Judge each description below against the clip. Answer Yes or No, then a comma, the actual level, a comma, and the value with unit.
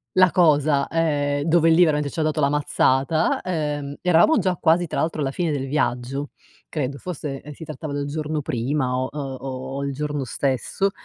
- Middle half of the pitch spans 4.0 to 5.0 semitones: No, narrow, 2.6 semitones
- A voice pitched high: No, medium, 150 Hz